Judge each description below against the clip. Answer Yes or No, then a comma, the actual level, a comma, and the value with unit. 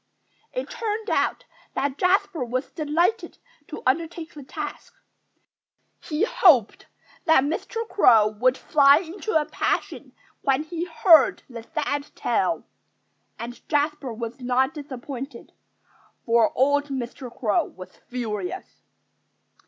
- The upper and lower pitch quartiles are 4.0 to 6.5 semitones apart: Yes, average, 4.8 semitones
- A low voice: No, very high, 285 Hz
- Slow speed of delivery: Yes, slow, 115 wpm